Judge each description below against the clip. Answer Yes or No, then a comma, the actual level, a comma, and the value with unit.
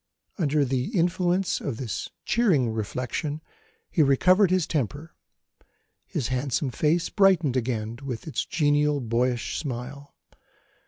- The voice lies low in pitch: No, medium, 145 Hz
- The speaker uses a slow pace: Yes, slow, 115 wpm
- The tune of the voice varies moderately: Yes, average, 4.8 semitones